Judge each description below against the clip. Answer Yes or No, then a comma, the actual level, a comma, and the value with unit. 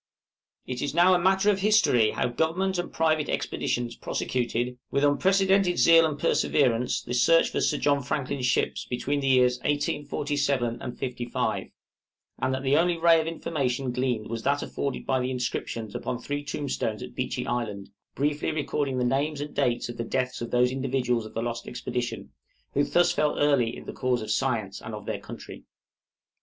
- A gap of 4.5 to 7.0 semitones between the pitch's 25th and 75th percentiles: No, average, 3.6 semitones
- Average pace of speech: Yes, average, 180 wpm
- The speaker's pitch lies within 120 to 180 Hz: Yes, low, 135 Hz